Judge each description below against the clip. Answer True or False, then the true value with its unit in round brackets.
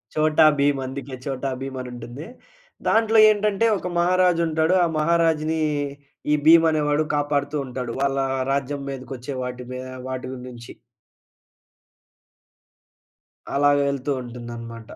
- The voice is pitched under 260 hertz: True (140 Hz)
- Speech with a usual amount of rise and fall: True (3.7 semitones)